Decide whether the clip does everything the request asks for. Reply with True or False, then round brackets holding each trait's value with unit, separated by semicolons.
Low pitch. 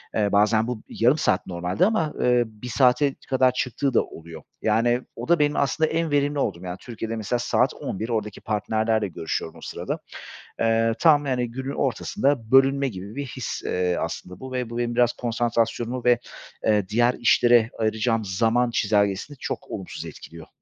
True (120 Hz)